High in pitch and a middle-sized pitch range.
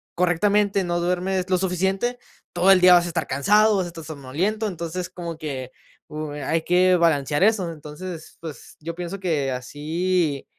No: medium, 175 Hz; average, 3.2 semitones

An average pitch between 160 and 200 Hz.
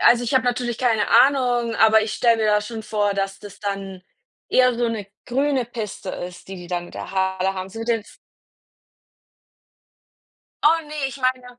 No: high, 225 Hz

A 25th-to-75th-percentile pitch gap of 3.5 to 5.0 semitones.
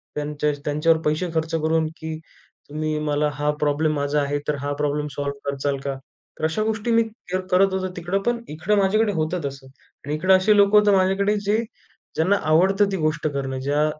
Yes: average, 4.7 semitones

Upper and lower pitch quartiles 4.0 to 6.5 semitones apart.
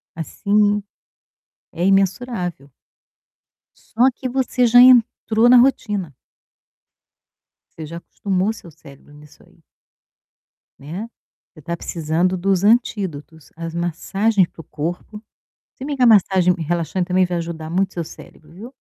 Yes: average, 4.9 semitones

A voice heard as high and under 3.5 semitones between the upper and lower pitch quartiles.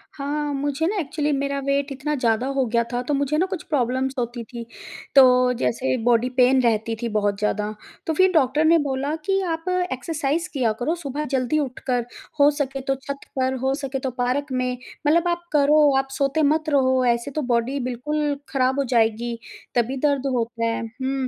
Yes: very high, 270 Hz; average, 3.1 semitones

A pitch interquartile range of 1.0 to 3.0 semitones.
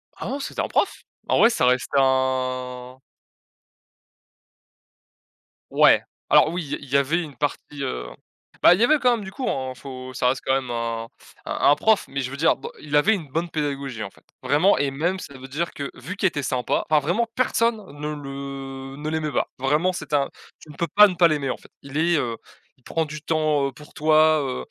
No: average, 3.8 semitones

